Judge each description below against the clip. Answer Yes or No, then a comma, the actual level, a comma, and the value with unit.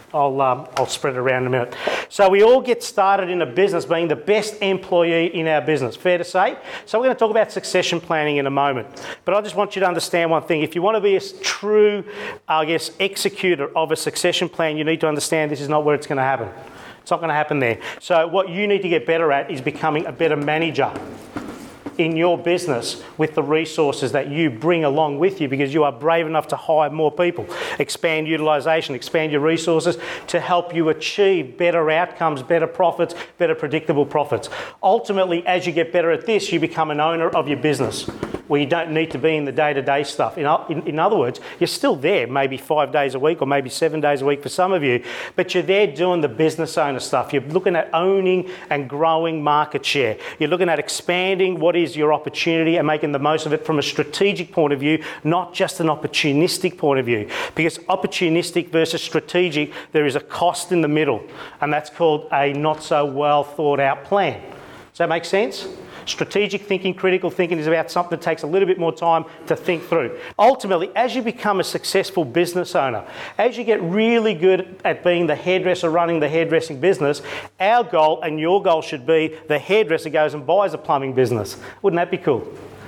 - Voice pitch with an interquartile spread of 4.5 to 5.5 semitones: No, average, 3.3 semitones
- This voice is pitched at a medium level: Yes, medium, 165 Hz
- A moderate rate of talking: No, fast, 220 wpm